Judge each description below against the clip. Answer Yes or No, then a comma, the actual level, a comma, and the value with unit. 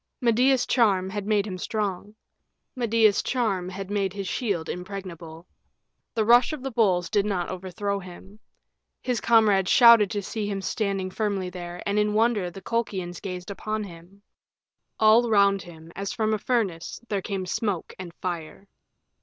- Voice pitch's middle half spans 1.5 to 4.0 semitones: Yes, average, 2.9 semitones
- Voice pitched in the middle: No, high, 200 Hz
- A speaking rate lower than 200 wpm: Yes, average, 160 wpm